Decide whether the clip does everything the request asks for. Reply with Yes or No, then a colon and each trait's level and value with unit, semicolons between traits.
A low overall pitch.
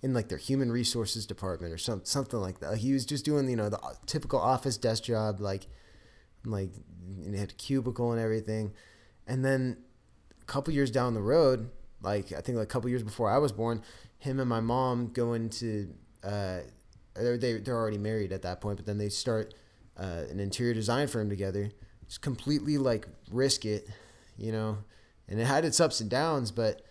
Yes: low, 110 Hz